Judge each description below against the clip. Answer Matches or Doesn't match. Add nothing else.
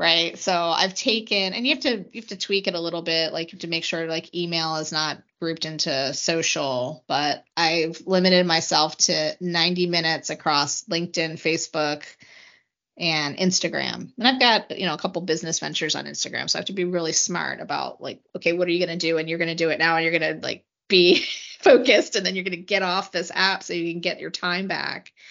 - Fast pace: Matches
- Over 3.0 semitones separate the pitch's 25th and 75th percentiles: Doesn't match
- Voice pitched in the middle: Matches